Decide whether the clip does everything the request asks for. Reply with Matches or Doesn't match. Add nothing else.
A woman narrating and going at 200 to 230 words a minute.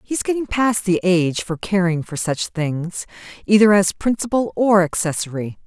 Doesn't match